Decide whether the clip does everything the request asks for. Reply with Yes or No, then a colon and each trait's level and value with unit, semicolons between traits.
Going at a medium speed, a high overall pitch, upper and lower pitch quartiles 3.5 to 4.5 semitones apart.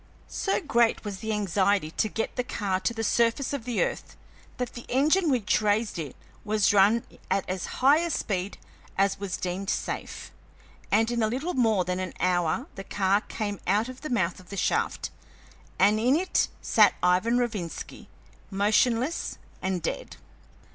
Yes: average, 170 wpm; high, 210 Hz; average, 4.1 semitones